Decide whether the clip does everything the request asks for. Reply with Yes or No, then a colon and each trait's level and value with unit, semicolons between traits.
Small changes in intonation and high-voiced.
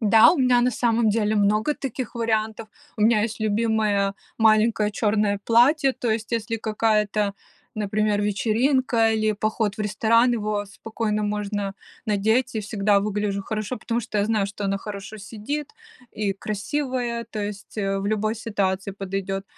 Yes: narrow, 1.9 semitones; high, 215 Hz